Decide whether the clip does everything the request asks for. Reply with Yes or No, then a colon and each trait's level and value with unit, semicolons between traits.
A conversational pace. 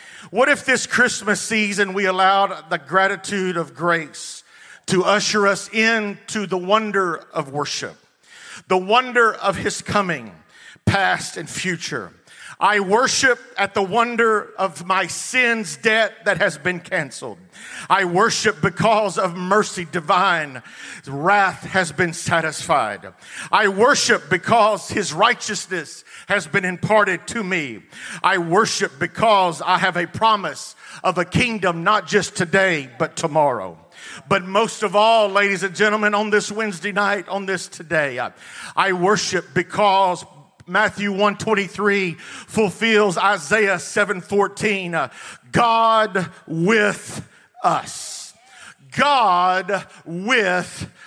No: slow, 120 wpm